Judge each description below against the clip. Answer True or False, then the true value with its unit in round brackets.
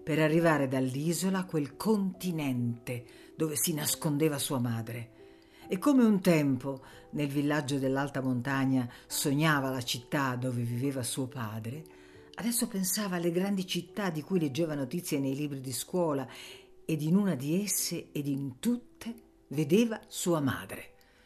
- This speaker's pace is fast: False (140 wpm)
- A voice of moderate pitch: True (150 Hz)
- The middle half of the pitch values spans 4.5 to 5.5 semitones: True (5.1 semitones)